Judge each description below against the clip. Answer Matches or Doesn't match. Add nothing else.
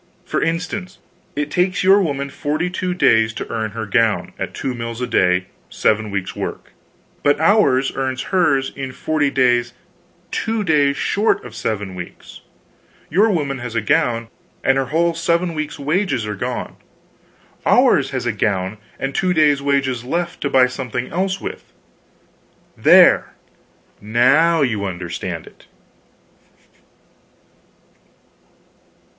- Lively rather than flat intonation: Matches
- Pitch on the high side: Doesn't match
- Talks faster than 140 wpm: Doesn't match